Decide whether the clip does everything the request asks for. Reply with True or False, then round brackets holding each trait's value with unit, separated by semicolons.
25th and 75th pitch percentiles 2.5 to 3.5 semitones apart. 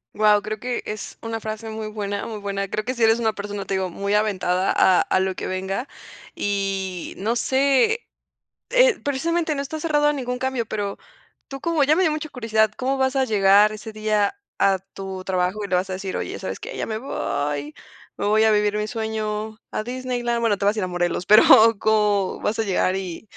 False (3.9 semitones)